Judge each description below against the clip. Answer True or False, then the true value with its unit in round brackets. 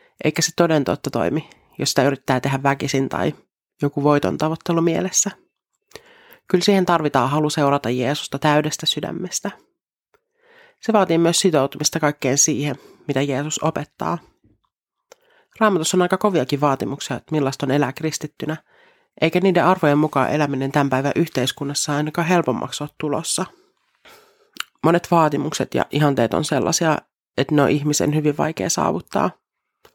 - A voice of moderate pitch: True (150 Hz)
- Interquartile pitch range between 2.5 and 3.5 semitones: False (4.1 semitones)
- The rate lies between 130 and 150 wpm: True (135 wpm)